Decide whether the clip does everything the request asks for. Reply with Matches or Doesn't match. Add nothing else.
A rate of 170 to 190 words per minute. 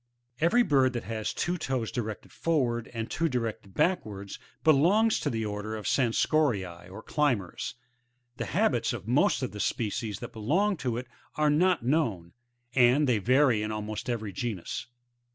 Doesn't match